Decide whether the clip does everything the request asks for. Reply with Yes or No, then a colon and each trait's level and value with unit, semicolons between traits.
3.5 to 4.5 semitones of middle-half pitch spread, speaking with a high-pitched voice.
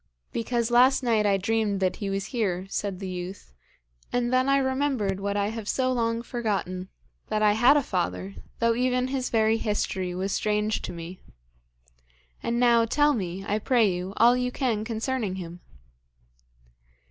Yes: average, 4.0 semitones; high, 220 Hz